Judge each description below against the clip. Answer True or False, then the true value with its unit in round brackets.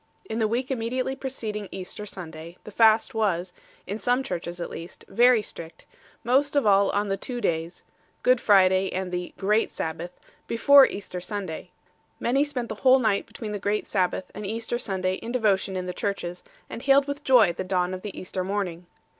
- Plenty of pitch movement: False (4.6 semitones)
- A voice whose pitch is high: True (205 Hz)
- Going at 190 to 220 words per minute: True (195 wpm)